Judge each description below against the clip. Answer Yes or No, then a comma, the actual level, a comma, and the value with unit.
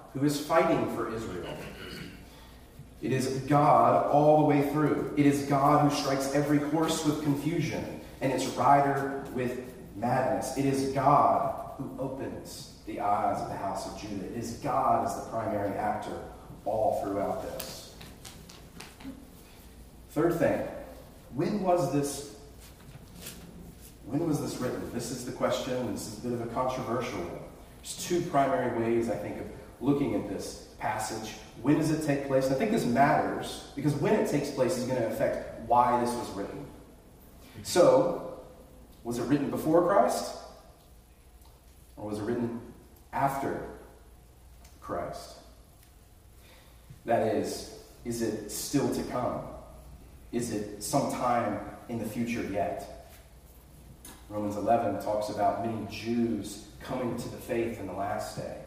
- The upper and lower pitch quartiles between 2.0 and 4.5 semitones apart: No, wide, 5.4 semitones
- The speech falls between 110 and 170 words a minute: Yes, average, 145 wpm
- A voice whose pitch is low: Yes, low, 120 Hz